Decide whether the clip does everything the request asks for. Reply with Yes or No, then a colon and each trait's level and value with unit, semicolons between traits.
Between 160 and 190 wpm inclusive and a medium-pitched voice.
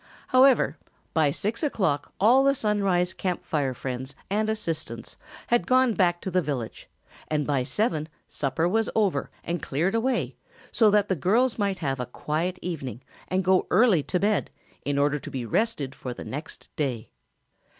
Yes: average, 170 wpm; medium, 180 Hz